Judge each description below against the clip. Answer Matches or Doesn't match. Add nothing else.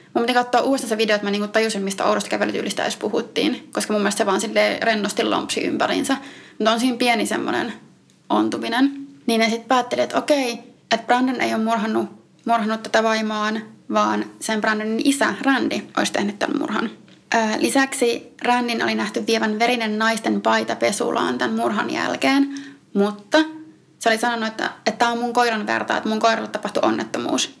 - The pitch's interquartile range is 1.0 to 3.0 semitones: Matches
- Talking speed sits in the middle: Doesn't match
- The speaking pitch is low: Doesn't match